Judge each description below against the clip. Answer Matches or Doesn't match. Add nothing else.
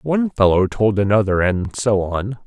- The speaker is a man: Matches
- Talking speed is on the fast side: Doesn't match